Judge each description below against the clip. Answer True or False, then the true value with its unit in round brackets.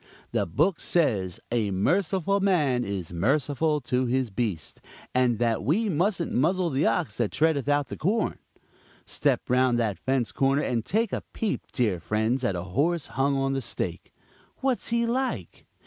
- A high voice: False (135 Hz)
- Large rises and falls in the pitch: True (6.7 semitones)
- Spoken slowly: False (165 wpm)